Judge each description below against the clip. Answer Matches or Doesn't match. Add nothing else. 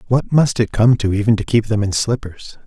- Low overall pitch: Matches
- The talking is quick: Matches